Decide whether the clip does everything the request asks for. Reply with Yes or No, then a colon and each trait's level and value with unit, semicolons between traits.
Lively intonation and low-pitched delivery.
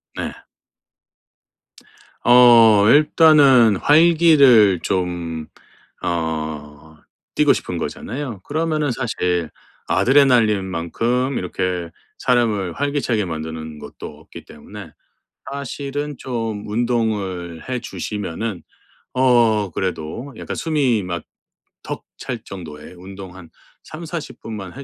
Yes: wide, 6.9 semitones; low, 110 Hz